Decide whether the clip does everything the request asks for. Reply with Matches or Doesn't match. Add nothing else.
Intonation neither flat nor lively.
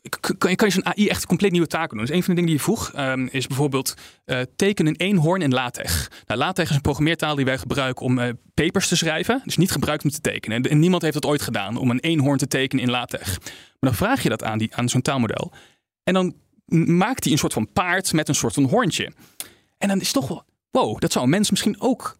Doesn't match